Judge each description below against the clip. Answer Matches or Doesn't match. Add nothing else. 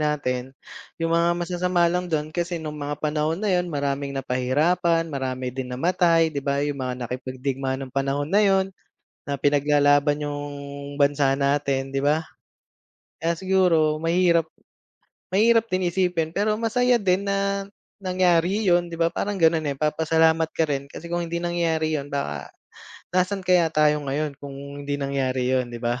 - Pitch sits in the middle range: Matches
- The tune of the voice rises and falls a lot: Doesn't match